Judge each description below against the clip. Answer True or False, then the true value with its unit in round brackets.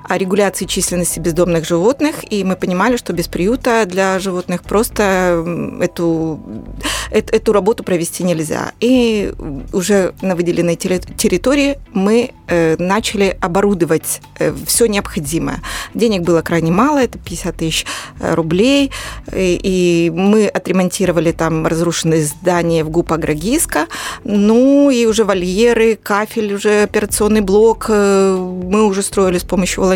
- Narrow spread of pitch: False (3.8 semitones)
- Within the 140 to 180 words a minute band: False (120 wpm)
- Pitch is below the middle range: False (190 Hz)